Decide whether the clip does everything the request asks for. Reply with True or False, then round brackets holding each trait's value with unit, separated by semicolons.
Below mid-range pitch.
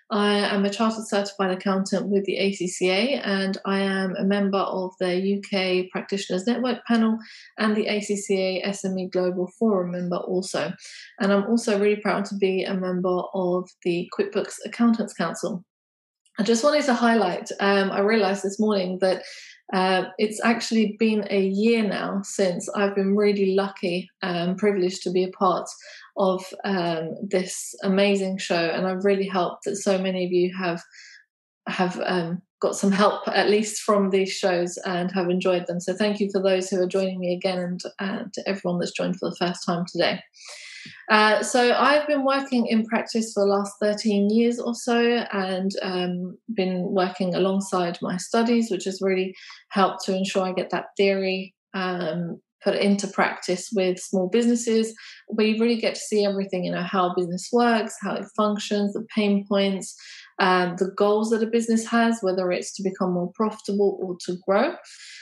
False (195 Hz)